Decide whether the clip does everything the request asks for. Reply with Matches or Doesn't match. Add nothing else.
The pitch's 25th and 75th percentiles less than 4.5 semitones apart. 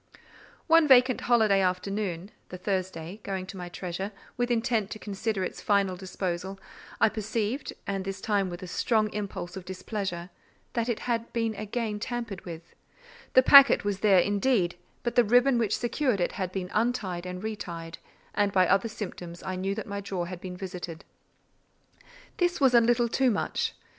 Matches